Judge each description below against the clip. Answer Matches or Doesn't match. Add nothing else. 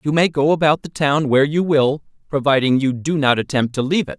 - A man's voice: Matches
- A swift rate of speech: Matches